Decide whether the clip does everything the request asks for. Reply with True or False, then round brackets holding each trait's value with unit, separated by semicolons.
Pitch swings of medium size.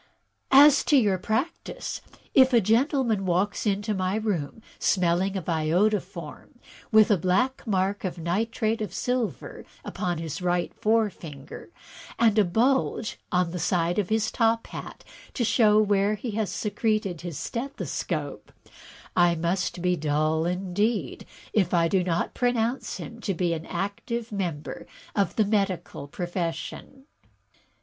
True (4.2 semitones)